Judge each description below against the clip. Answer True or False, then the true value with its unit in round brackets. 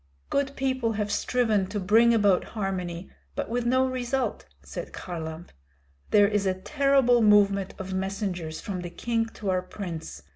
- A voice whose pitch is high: True (205 Hz)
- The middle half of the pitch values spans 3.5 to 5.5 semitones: True (4.2 semitones)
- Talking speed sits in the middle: True (155 wpm)